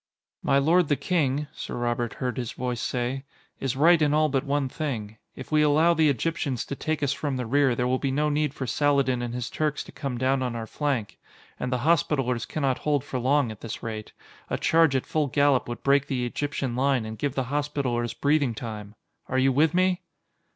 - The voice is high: No, low, 135 Hz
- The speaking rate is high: Yes, fast, 215 wpm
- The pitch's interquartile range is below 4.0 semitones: Yes, average, 3.1 semitones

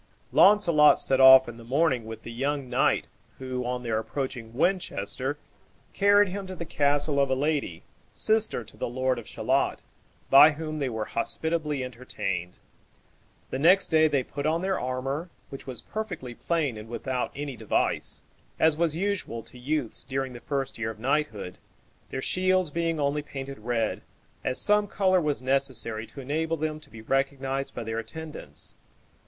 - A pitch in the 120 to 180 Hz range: Yes, low, 135 Hz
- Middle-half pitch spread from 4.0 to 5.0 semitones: Yes, average, 4.4 semitones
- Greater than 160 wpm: Yes, average, 170 wpm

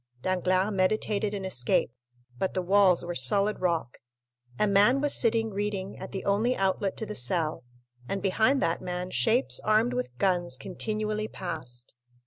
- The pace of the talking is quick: No, average, 155 wpm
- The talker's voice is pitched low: No, high, 195 Hz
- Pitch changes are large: No, average, 3.1 semitones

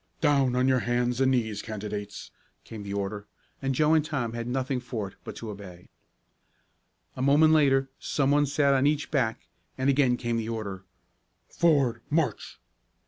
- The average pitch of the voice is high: No, low, 125 Hz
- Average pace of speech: Yes, average, 170 wpm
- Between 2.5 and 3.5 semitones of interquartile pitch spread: No, average, 4.2 semitones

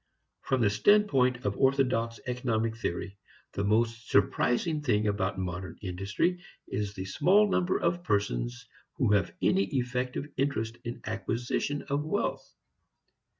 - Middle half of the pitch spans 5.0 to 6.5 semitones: Yes, average, 5.3 semitones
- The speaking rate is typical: No, slow, 130 wpm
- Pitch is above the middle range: No, low, 115 Hz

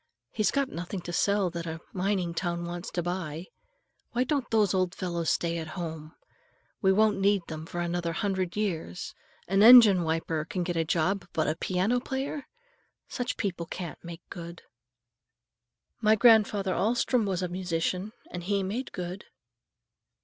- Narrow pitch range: No, average, 3.2 semitones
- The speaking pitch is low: No, medium, 185 Hz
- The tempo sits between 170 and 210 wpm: No, average, 160 wpm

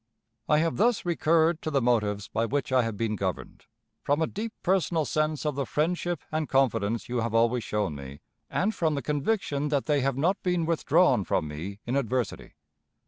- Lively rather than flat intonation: Yes, wide, 6.0 semitones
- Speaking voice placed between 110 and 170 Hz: Yes, medium, 140 Hz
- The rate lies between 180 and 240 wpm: Yes, average, 195 wpm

